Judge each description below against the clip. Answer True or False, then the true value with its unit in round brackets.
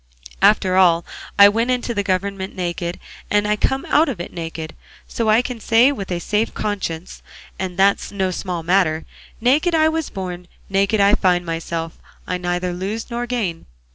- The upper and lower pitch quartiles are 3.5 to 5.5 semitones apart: True (4.2 semitones)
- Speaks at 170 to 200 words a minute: True (175 wpm)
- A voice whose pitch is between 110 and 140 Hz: False (195 Hz)